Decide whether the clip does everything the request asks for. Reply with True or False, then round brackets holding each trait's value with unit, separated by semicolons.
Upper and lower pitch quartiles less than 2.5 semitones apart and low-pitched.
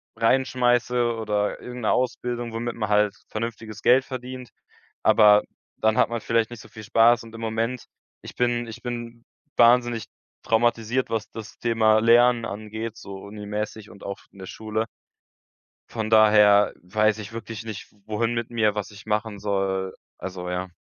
True (2.1 semitones; 110 Hz)